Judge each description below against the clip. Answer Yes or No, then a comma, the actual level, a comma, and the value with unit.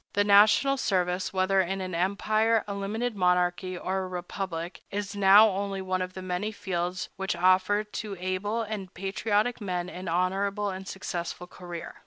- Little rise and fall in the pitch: Yes, narrow, 2.0 semitones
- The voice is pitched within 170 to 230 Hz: Yes, high, 190 Hz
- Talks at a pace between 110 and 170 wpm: Yes, average, 160 wpm